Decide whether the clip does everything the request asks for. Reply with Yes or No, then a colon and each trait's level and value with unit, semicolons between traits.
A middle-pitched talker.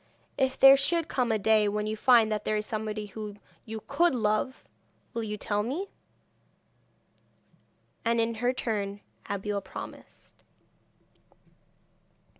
No: high, 220 Hz